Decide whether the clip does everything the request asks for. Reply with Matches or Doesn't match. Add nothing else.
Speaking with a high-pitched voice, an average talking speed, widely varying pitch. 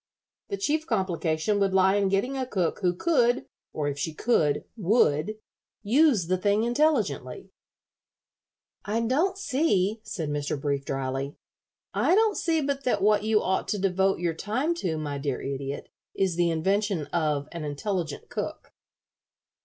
Matches